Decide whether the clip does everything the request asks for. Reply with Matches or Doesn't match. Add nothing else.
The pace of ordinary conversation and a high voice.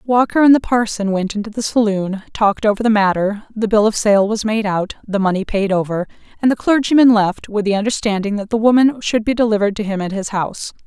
Doesn't match